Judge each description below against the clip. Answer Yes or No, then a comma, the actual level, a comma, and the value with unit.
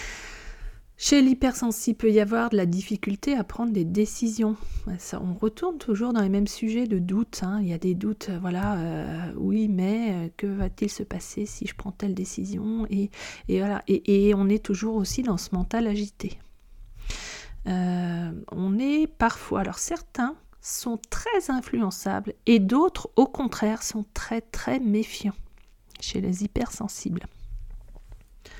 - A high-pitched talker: Yes, high, 210 Hz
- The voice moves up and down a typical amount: Yes, average, 3.2 semitones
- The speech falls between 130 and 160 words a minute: Yes, average, 155 wpm